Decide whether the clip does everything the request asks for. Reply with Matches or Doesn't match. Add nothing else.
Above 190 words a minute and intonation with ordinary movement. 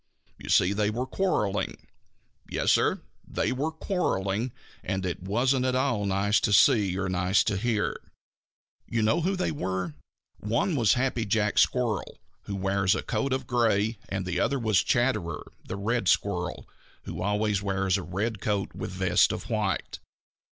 Doesn't match